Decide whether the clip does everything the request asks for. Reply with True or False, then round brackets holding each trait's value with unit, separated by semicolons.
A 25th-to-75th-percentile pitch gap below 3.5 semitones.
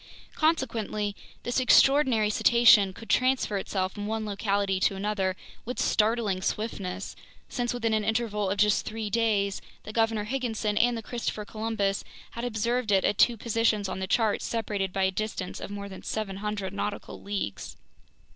True (2.4 semitones)